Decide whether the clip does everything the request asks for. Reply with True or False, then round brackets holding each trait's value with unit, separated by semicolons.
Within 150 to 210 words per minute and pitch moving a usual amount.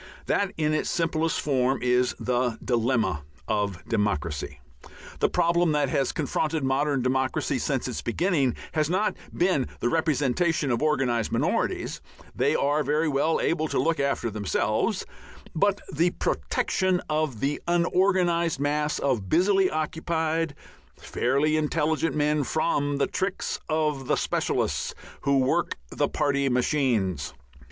False (135 wpm; 4.1 semitones)